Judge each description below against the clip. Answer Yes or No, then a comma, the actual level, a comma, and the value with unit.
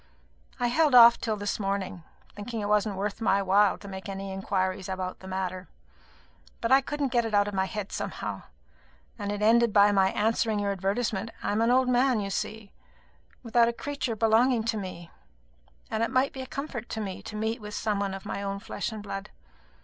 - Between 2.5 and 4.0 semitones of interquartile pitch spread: Yes, average, 3.0 semitones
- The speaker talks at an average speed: No, fast, 210 wpm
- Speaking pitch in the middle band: No, high, 210 Hz